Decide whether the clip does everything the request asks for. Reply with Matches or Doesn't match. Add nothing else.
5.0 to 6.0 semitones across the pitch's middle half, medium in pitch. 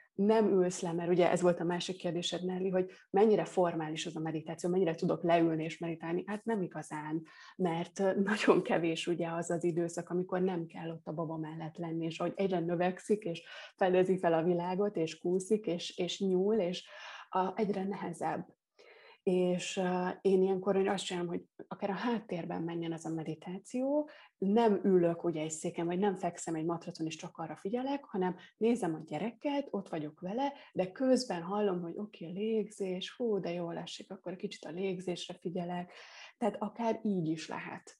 Doesn't match